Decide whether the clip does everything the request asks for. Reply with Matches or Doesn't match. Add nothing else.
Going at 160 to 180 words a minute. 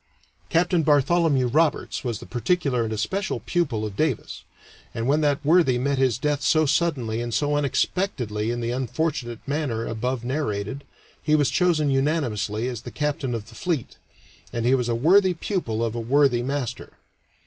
Matches